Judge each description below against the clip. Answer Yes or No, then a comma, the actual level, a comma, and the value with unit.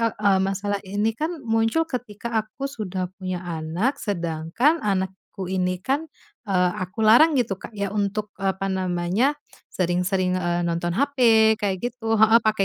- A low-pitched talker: No, high, 200 Hz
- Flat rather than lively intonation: No, average, 3.5 semitones